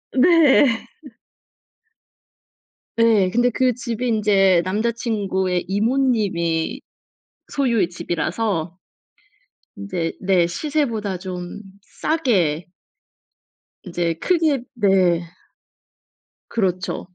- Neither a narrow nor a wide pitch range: Yes, average, 4.8 semitones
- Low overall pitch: No, high, 205 Hz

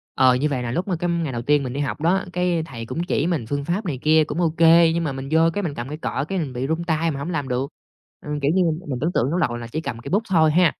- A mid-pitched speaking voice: Yes, medium, 155 Hz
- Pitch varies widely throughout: No, average, 4.1 semitones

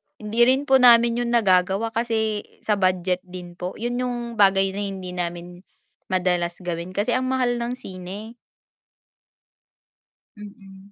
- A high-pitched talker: Yes, high, 200 Hz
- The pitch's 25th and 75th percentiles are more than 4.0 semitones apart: Yes, average, 4.4 semitones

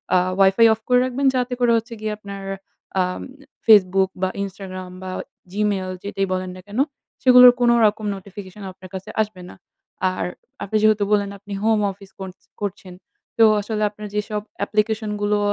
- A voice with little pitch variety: Yes, narrow, 2.2 semitones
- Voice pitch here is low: No, high, 205 Hz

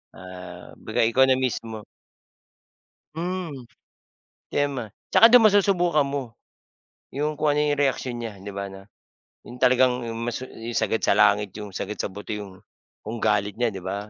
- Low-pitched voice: Yes, low, 120 Hz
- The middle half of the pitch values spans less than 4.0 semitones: No, wide, 5.6 semitones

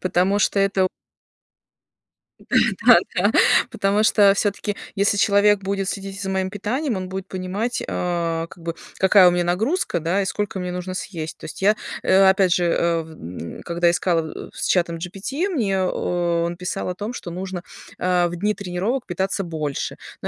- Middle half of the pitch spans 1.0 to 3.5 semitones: Yes, narrow, 2.4 semitones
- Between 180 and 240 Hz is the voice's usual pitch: Yes, medium, 185 Hz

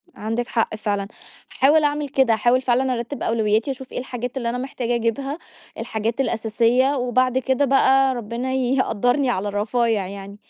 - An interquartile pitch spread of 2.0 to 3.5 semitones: Yes, average, 2.8 semitones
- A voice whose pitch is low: No, high, 245 Hz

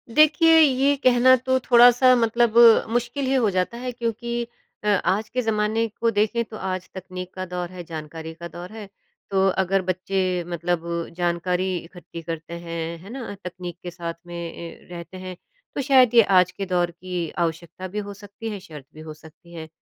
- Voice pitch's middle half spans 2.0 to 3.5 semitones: No, average, 5.3 semitones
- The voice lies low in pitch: No, medium, 185 Hz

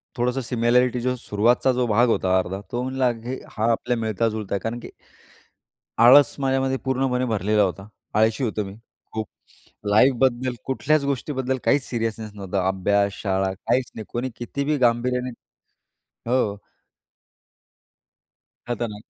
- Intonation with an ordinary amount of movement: Yes, average, 3.3 semitones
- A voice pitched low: Yes, low, 120 Hz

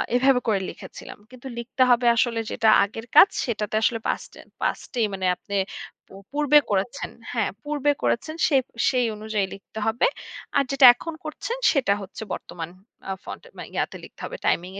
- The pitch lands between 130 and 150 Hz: No, high, 235 Hz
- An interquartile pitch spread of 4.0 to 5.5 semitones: Yes, average, 4.6 semitones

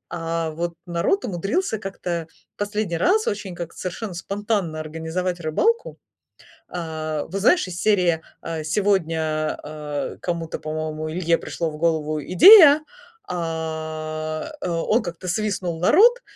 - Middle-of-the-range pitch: Yes, medium, 170 Hz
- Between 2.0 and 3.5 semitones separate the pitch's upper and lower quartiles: No, average, 3.9 semitones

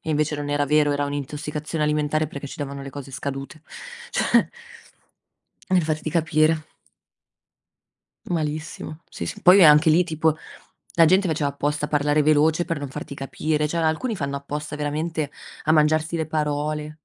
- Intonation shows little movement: Yes, narrow, 1.5 semitones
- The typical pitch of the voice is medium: Yes, medium, 150 Hz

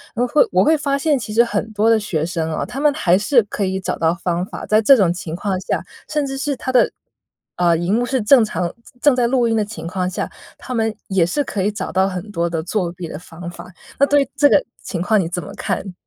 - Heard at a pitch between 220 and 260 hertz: No, high, 205 Hz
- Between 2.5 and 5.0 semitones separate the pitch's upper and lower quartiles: No, wide, 5.5 semitones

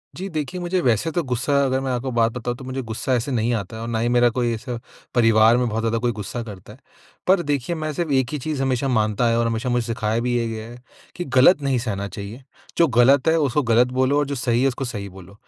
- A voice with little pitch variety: No, average, 3.0 semitones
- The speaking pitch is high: No, low, 120 Hz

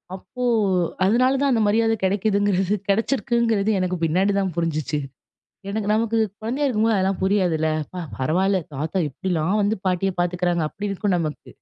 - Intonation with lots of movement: No, average, 3.5 semitones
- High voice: Yes, high, 195 Hz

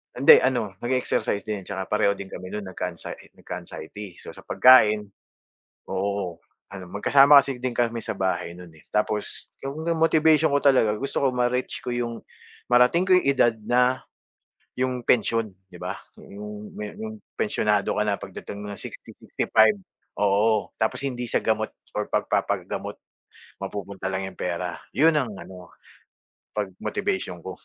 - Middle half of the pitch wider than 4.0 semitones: Yes, average, 4.4 semitones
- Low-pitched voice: Yes, low, 105 Hz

